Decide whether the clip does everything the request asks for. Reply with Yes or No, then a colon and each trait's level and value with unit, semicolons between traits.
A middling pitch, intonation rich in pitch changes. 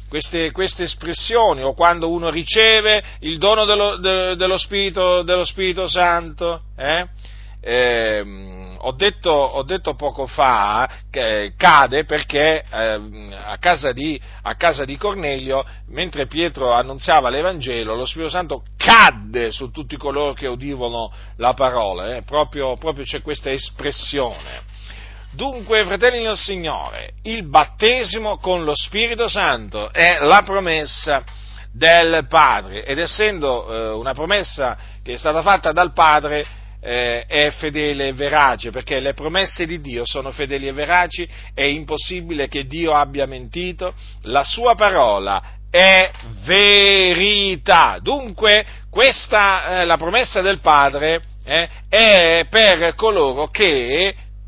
Yes: medium, 155 Hz; wide, 6.1 semitones